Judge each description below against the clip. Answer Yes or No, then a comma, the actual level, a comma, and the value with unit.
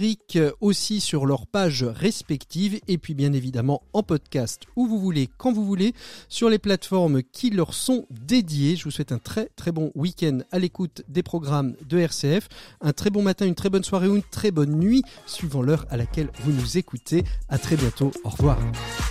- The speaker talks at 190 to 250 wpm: Yes, average, 200 wpm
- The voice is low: No, medium, 165 Hz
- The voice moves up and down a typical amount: No, wide, 6.1 semitones